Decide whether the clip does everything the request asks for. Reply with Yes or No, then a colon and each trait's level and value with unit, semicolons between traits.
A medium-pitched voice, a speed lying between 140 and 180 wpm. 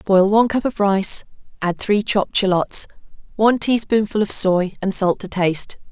No: high, 200 Hz; average, 170 wpm